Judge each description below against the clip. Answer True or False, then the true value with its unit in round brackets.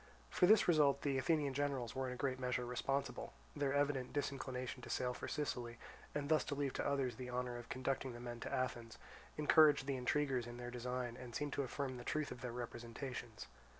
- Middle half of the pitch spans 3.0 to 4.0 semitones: False (2.5 semitones)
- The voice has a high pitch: False (130 Hz)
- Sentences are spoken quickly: True (210 wpm)